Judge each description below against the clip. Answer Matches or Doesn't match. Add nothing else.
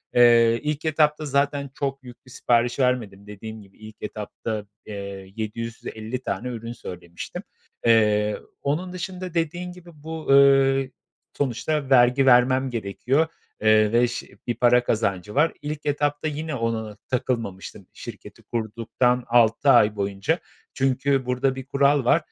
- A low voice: Matches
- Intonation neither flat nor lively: Matches